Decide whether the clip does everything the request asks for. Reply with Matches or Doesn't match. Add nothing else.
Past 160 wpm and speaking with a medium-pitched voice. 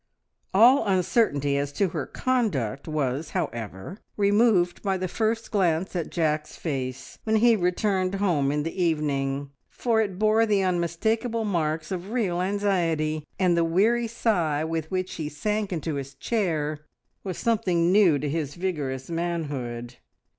Doesn't match